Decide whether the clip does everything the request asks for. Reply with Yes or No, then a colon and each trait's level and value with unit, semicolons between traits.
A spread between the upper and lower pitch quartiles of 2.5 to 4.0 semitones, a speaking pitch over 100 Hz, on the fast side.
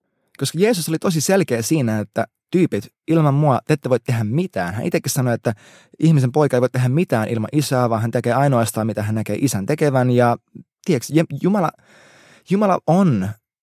No: average, 5.3 semitones; low, 135 Hz; fast, 180 wpm